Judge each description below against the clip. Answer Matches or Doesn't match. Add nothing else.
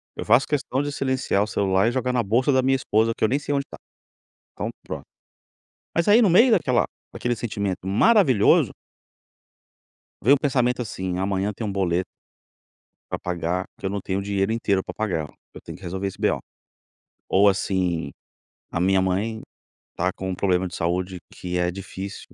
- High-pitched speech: Doesn't match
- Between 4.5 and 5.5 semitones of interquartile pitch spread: Matches